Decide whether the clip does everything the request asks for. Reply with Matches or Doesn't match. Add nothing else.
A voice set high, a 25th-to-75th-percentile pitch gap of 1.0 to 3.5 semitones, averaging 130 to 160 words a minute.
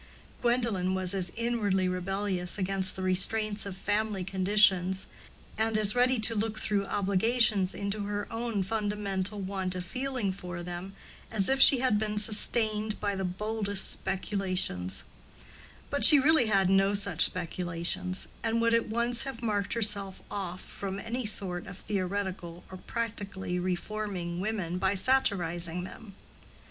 Matches